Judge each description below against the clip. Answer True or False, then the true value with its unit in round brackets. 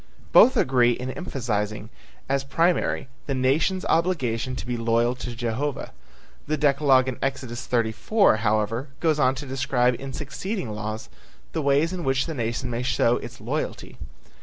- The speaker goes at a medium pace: True (155 wpm)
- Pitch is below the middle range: True (130 Hz)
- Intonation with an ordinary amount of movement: True (3.6 semitones)